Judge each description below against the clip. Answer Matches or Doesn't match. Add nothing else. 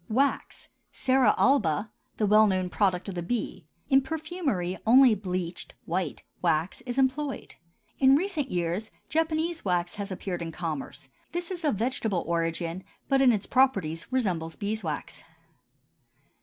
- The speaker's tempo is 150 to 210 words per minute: Doesn't match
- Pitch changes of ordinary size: Doesn't match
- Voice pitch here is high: Matches